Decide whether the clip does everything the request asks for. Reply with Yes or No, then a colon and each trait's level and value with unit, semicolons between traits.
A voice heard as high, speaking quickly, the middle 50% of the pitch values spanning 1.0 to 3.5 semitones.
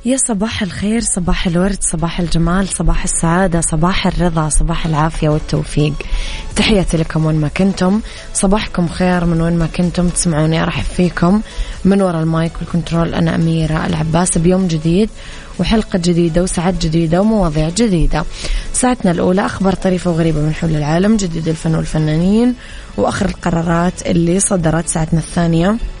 No: medium, 175 Hz; fast, 140 wpm; narrow, 2.6 semitones